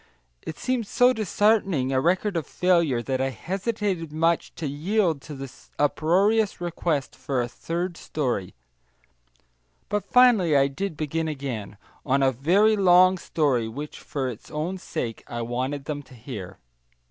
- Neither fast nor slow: Yes, average, 150 wpm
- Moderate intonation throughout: No, wide, 5.7 semitones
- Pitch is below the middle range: No, medium, 155 Hz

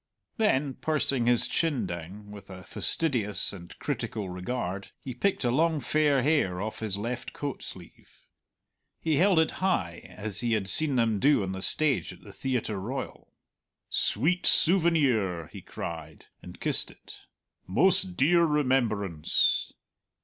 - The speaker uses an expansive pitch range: Yes, wide, 7.6 semitones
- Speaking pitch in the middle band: No, low, 120 Hz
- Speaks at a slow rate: No, average, 145 wpm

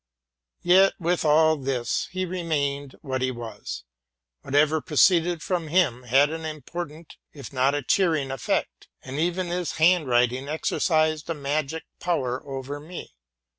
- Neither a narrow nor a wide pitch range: Yes, average, 3.8 semitones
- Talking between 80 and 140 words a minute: Yes, slow, 135 wpm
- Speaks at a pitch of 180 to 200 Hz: No, medium, 155 Hz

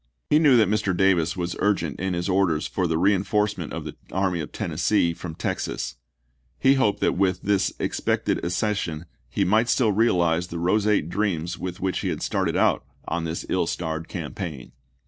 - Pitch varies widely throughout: No, average, 3.4 semitones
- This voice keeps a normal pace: Yes, average, 180 wpm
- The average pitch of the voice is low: Yes, very low, 90 Hz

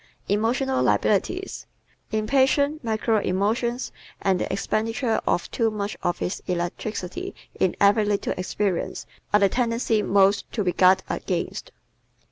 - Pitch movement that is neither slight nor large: Yes, average, 3.2 semitones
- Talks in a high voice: Yes, high, 210 Hz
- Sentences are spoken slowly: Yes, slow, 130 wpm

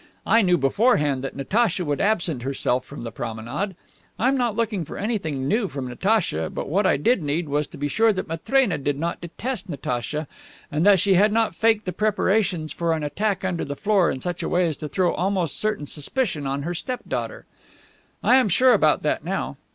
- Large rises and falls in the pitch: Yes, wide, 6.7 semitones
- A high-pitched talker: No, medium, 175 Hz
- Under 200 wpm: No, fast, 205 wpm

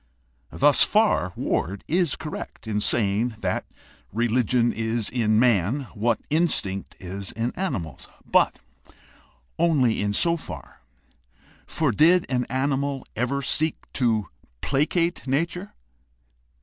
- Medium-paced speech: No, slow, 110 wpm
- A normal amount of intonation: No, wide, 5.8 semitones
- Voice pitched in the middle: No, low, 125 Hz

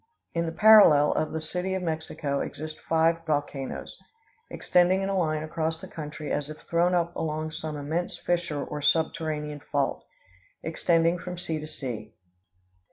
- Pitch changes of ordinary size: No, narrow, 2.3 semitones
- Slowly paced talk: No, average, 160 wpm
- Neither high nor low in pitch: Yes, medium, 160 Hz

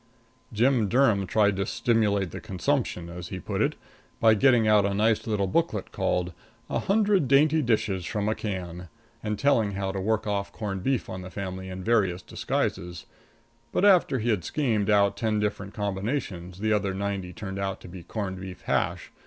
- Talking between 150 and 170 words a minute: No, average, 185 wpm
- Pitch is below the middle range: Yes, low, 100 Hz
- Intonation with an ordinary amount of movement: Yes, average, 3.1 semitones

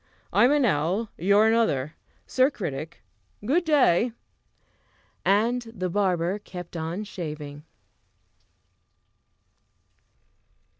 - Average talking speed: No, slow, 85 wpm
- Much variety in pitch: Yes, wide, 5.7 semitones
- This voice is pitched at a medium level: No, high, 200 Hz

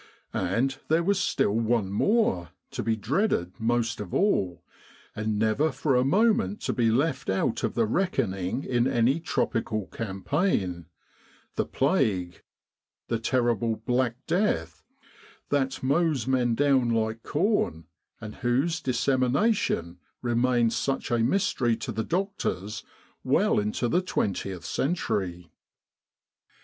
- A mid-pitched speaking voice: No, low, 120 Hz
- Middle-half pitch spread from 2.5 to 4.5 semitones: No, average, 5.1 semitones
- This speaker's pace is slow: Yes, slow, 125 wpm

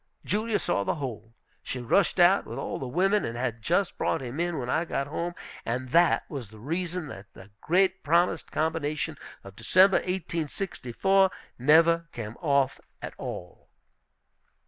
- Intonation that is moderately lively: No, wide, 6.1 semitones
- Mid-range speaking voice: Yes, medium, 155 Hz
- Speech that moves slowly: No, average, 160 wpm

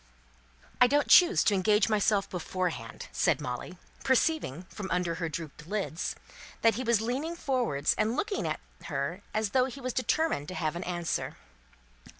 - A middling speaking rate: Yes, average, 160 wpm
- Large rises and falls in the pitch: Yes, wide, 6.7 semitones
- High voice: Yes, high, 210 Hz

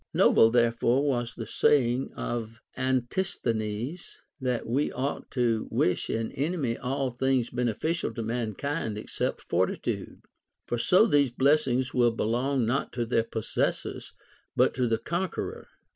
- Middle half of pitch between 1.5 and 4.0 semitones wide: Yes, average, 2.9 semitones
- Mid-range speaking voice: No, low, 125 Hz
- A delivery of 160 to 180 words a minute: No, average, 140 wpm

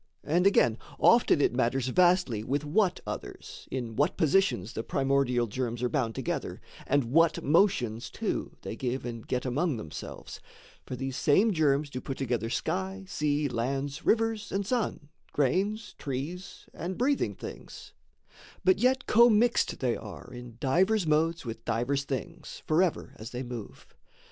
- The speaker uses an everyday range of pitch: No, wide, 6.9 semitones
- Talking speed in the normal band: Yes, average, 150 wpm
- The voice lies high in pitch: No, medium, 140 Hz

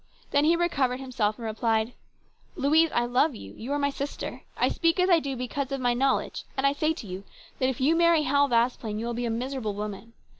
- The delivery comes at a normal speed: No, fast, 235 wpm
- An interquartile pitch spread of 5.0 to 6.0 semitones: No, average, 3.7 semitones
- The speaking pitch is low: No, very high, 260 Hz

